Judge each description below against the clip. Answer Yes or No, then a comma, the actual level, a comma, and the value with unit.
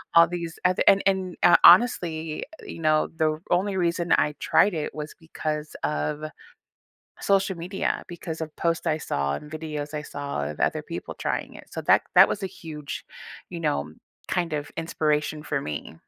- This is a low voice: No, medium, 160 Hz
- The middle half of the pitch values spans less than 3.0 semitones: Yes, narrow, 2.5 semitones